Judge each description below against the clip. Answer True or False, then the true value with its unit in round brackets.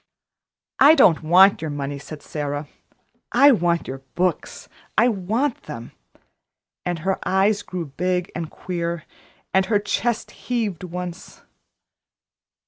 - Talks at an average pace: False (125 wpm)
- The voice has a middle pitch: True (180 Hz)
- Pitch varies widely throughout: False (4.2 semitones)